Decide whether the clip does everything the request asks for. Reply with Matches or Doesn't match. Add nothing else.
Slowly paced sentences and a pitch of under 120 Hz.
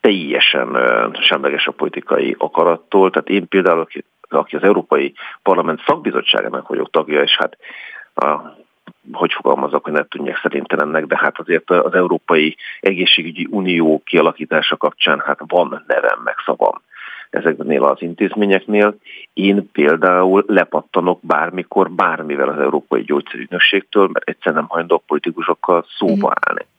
Doesn't match